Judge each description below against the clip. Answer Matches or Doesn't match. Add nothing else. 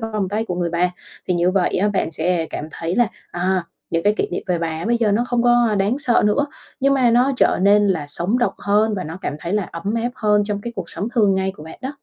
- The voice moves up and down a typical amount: Matches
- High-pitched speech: Matches